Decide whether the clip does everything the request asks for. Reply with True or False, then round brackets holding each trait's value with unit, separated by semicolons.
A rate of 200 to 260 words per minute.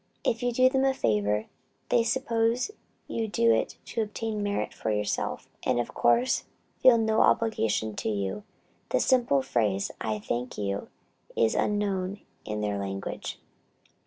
False (150 wpm)